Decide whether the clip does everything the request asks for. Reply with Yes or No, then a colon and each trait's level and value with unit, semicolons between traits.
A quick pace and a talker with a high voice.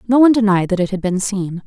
Yes: fast, 290 wpm; high, 200 Hz